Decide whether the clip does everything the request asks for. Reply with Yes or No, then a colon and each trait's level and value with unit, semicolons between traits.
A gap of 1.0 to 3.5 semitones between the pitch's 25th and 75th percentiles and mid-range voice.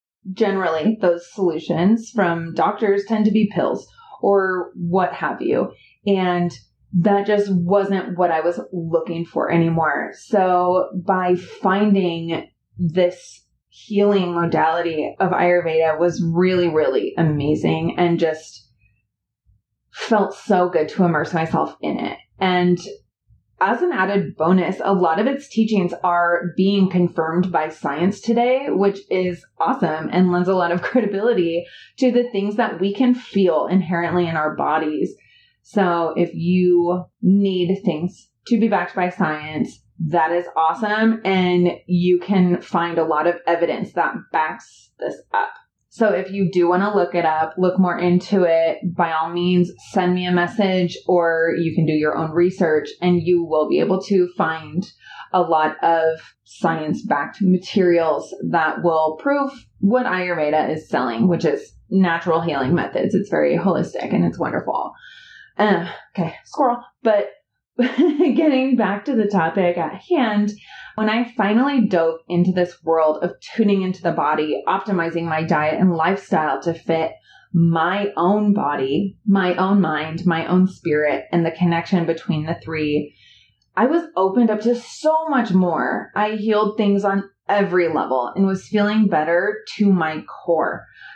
Yes: average, 3.1 semitones; medium, 180 Hz